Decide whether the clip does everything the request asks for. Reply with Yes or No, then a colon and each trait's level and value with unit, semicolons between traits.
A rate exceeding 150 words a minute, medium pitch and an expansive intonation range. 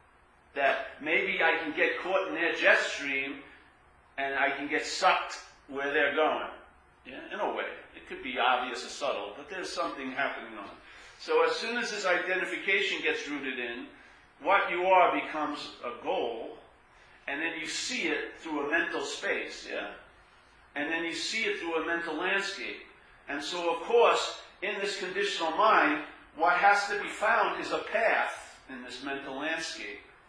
Yes: average, 175 wpm; medium, 165 Hz; wide, 6.1 semitones